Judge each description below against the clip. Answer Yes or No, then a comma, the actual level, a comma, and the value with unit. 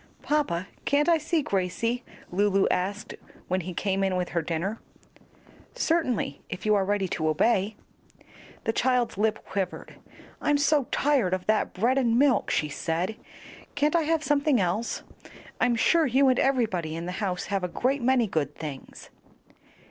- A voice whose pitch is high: Yes, high, 215 Hz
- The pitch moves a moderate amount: No, wide, 6.6 semitones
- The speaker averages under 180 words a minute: Yes, average, 165 wpm